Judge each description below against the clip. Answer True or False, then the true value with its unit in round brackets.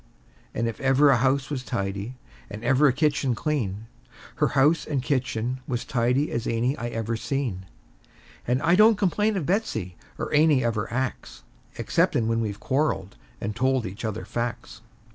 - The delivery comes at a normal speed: True (170 wpm)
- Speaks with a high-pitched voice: False (125 Hz)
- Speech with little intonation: False (4.0 semitones)